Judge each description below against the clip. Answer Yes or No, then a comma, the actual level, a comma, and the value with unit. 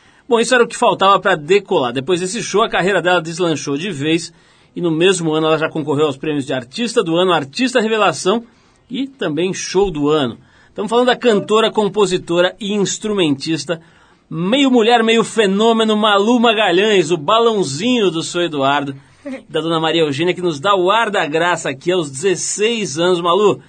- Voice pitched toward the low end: No, medium, 185 Hz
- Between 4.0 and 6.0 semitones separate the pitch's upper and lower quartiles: Yes, average, 5.3 semitones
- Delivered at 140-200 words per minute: Yes, average, 180 wpm